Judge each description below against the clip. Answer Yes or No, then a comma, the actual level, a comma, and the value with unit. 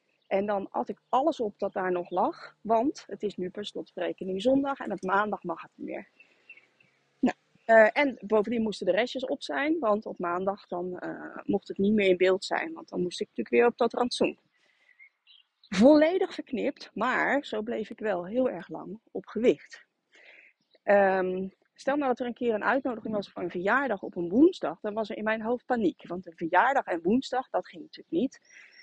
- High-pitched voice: Yes, high, 220 Hz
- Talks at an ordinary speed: No, fast, 205 wpm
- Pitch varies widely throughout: Yes, wide, 5.8 semitones